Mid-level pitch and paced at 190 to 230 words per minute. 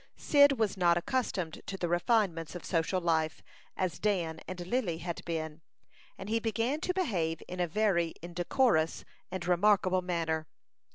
No: medium, 180 Hz; average, 155 wpm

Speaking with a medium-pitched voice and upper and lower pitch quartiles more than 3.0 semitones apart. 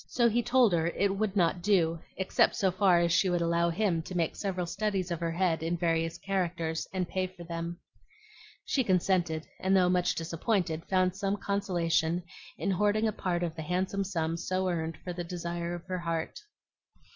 No: medium, 180 Hz; narrow, 2.4 semitones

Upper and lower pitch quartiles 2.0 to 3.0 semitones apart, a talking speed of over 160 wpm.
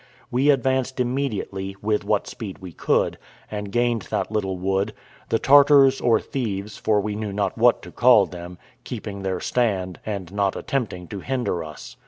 No: average, 4.2 semitones; average, 170 wpm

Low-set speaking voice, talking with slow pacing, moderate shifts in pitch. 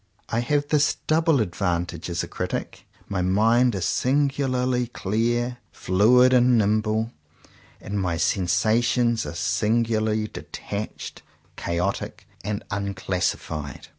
Yes: low, 110 Hz; slow, 115 wpm; average, 4.6 semitones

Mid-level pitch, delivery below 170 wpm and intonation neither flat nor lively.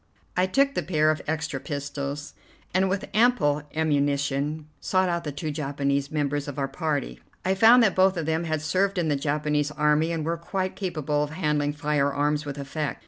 No: medium, 150 Hz; average, 190 wpm; average, 3.0 semitones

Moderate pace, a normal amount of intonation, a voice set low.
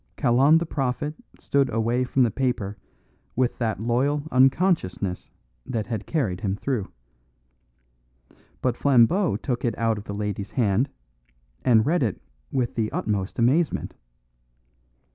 No: slow, 130 wpm; average, 4.1 semitones; low, 120 Hz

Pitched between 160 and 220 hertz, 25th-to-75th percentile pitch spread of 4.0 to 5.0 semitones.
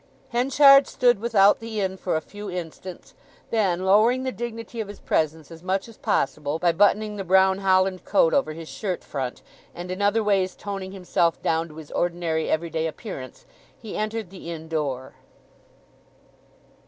Yes: high, 190 Hz; average, 4.3 semitones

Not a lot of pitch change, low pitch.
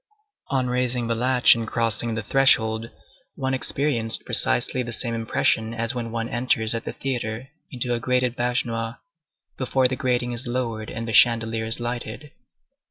Yes: narrow, 1.9 semitones; low, 120 Hz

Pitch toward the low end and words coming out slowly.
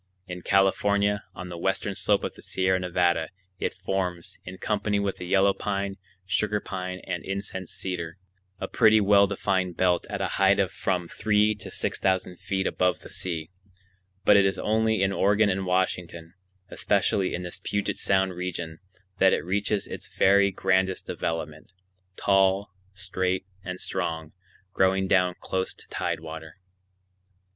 No: very low, 95 Hz; average, 150 wpm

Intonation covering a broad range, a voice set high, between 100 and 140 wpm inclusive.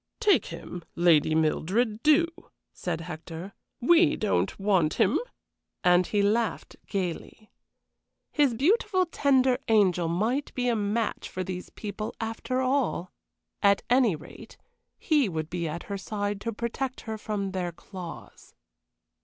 Yes: wide, 5.8 semitones; high, 205 Hz; slow, 135 wpm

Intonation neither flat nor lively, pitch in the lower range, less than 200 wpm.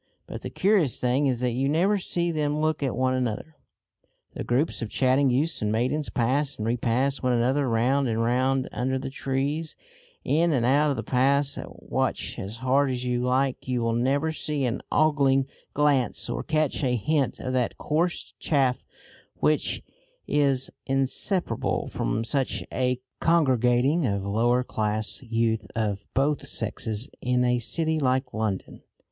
Yes: average, 3.1 semitones; low, 130 Hz; average, 165 wpm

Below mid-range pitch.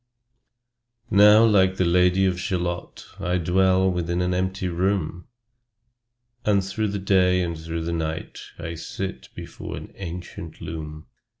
Yes: very low, 90 Hz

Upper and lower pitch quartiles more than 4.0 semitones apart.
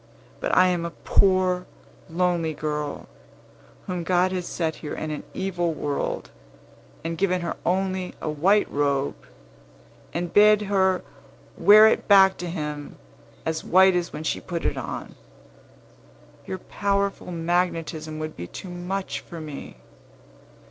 No: average, 3.0 semitones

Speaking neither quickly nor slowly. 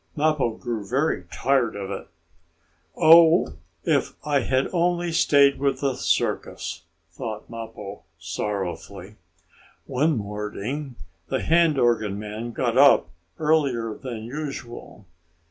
No: slow, 110 wpm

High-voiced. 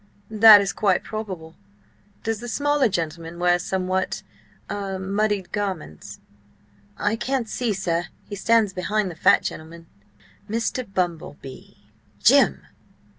Yes: high, 195 Hz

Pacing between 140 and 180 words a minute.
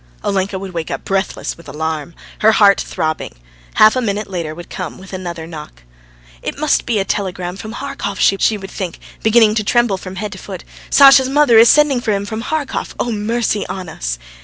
No: average, 195 wpm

